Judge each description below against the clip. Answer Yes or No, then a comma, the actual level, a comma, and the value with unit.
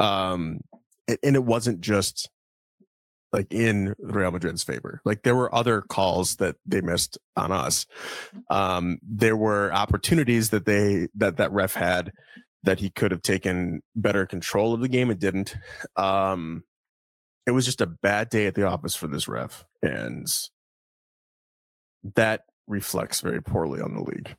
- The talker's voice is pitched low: Yes, low, 100 Hz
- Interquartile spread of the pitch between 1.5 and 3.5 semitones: Yes, average, 3.2 semitones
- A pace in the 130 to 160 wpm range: Yes, average, 155 wpm